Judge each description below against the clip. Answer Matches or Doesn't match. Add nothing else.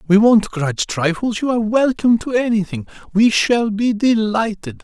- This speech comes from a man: Matches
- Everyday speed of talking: Matches